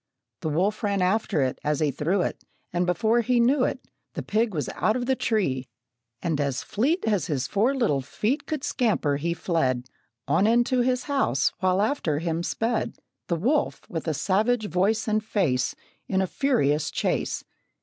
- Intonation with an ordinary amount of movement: No, wide, 7.2 semitones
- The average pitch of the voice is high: Yes, high, 195 Hz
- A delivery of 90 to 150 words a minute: No, average, 180 wpm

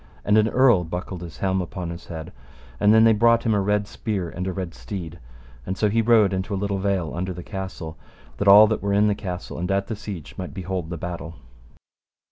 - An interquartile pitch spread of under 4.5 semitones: Yes, average, 2.8 semitones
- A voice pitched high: No, very low, 95 Hz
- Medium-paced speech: No, fast, 230 wpm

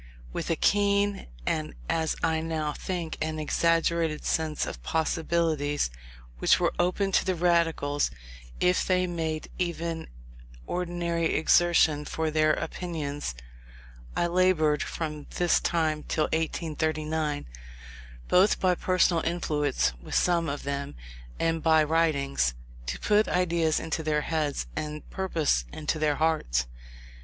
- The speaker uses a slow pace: Yes, slow, 130 wpm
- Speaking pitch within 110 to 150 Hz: No, medium, 160 Hz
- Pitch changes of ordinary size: No, narrow, 2.1 semitones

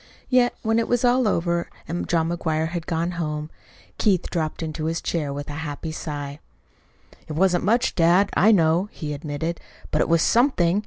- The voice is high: No, medium, 170 Hz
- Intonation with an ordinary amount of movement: Yes, average, 3.5 semitones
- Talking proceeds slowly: No, average, 180 wpm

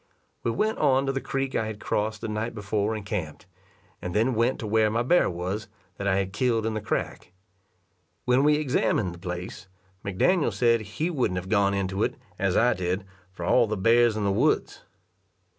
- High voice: No, low, 110 Hz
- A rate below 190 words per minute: No, average, 200 wpm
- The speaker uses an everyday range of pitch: Yes, average, 3.7 semitones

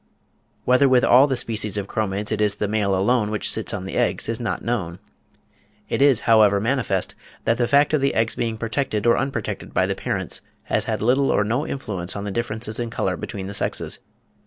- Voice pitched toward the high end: No, low, 110 Hz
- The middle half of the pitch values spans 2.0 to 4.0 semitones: Yes, average, 3.4 semitones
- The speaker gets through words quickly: Yes, fast, 210 wpm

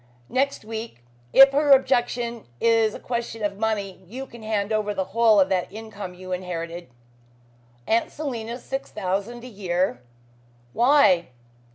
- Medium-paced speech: Yes, average, 150 wpm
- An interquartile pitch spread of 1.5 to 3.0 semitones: No, average, 3.9 semitones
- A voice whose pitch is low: No, high, 220 Hz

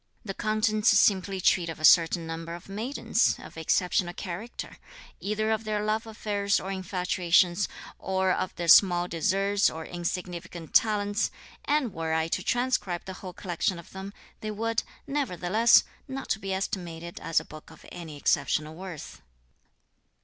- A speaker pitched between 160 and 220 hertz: Yes, high, 190 Hz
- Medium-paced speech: Yes, average, 150 wpm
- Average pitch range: Yes, average, 3.6 semitones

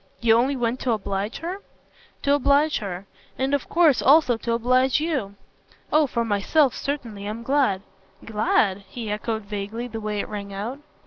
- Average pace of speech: Yes, average, 170 wpm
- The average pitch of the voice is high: Yes, high, 235 Hz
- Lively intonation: No, average, 5.0 semitones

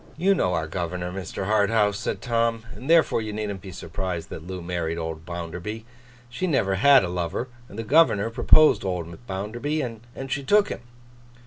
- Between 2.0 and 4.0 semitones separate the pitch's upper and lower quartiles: No, average, 5.3 semitones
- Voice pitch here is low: Yes, low, 100 Hz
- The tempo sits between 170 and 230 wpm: Yes, average, 180 wpm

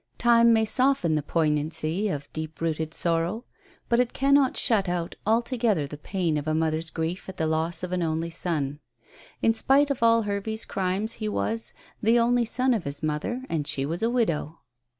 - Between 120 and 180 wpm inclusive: No, average, 190 wpm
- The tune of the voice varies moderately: No, wide, 6.4 semitones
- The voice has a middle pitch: Yes, medium, 180 Hz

